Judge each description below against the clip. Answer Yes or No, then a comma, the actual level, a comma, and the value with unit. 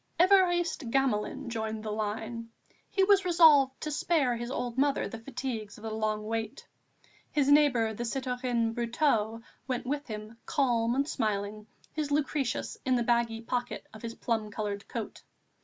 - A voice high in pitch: Yes, high, 240 Hz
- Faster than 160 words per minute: No, average, 155 wpm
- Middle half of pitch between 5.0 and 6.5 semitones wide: No, average, 4.1 semitones